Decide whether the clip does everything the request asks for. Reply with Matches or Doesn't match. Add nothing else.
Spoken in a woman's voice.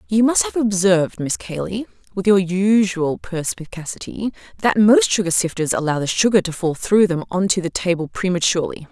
Matches